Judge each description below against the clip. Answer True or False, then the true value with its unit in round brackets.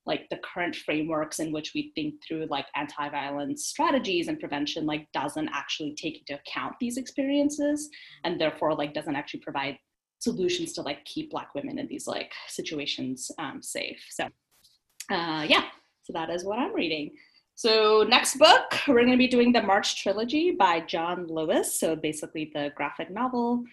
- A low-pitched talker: False (230 Hz)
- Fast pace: False (170 wpm)